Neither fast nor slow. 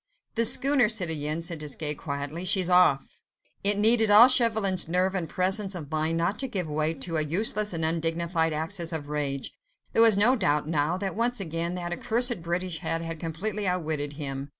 Yes: average, 185 wpm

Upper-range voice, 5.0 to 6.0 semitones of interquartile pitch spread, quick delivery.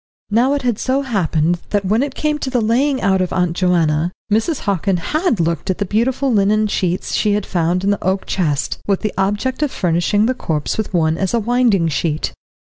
Yes: high, 200 Hz; wide, 5.5 semitones; fast, 215 wpm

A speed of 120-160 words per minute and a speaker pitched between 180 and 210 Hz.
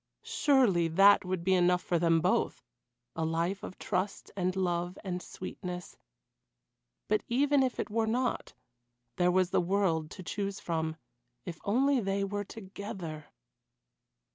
Yes: average, 140 wpm; medium, 185 Hz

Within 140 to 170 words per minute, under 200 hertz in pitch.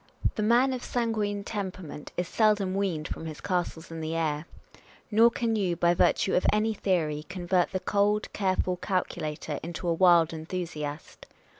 Yes: average, 160 wpm; medium, 185 Hz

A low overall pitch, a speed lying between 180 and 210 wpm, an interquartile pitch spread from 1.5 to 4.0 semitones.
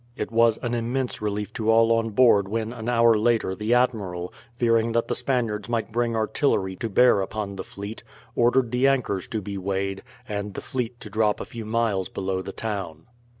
Yes: low, 110 Hz; average, 195 wpm; average, 2.7 semitones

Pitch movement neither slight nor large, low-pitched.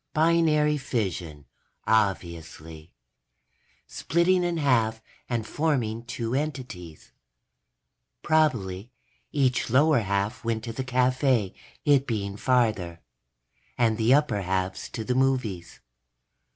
No: wide, 5.8 semitones; low, 115 Hz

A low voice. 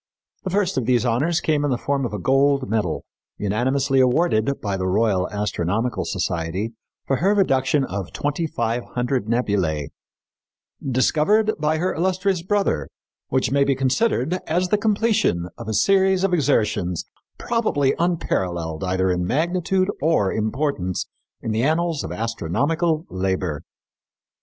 Yes: low, 130 Hz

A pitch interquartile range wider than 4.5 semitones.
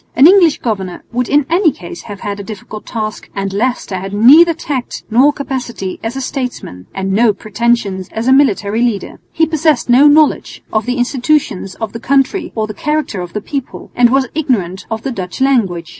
Yes: wide, 5.5 semitones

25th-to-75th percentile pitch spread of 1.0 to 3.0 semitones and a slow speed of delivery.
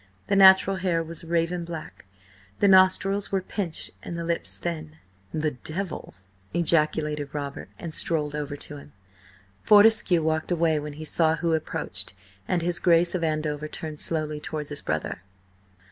No: narrow, 2.5 semitones; average, 155 wpm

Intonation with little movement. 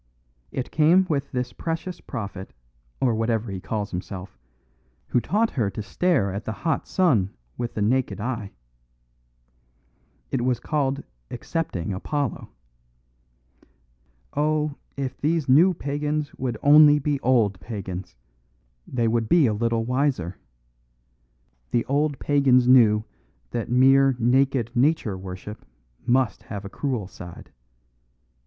No: average, 5.3 semitones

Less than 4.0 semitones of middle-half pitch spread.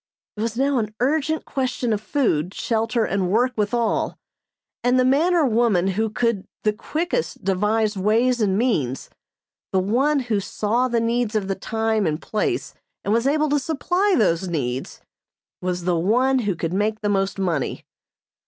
No: average, 4.6 semitones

